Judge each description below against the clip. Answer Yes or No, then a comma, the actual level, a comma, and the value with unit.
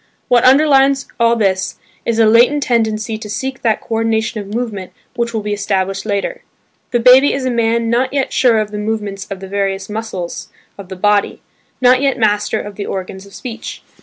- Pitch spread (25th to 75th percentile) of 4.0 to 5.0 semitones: No, average, 3.1 semitones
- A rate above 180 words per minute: Yes, average, 195 wpm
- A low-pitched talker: No, high, 220 Hz